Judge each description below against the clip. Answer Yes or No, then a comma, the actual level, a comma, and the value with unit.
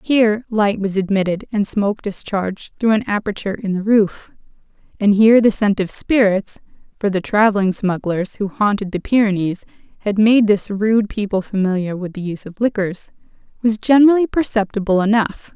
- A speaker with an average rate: Yes, average, 160 wpm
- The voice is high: Yes, high, 205 Hz